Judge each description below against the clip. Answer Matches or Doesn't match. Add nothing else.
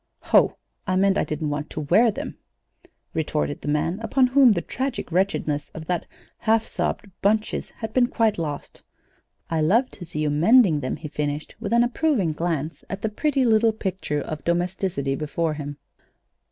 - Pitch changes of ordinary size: Doesn't match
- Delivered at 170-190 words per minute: Matches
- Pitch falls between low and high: Matches